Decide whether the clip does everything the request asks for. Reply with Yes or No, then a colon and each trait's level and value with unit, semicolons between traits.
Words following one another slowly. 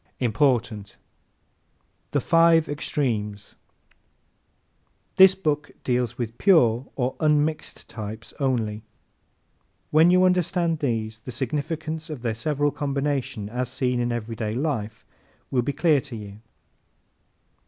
Yes: slow, 115 wpm